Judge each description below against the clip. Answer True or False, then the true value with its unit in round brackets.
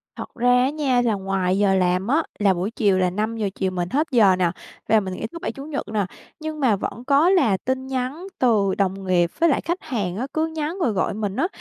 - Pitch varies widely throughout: True (6.3 semitones)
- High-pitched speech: True (220 Hz)